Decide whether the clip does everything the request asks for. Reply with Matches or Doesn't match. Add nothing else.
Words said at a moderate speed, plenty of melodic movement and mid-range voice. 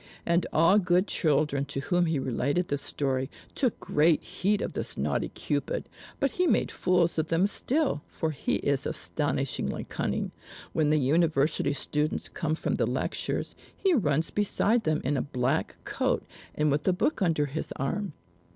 Doesn't match